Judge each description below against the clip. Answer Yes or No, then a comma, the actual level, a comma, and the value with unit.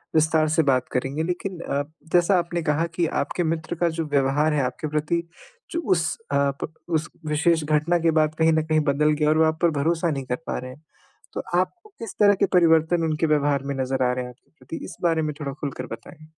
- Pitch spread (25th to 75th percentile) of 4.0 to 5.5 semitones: No, average, 2.9 semitones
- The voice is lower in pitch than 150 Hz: No, medium, 155 Hz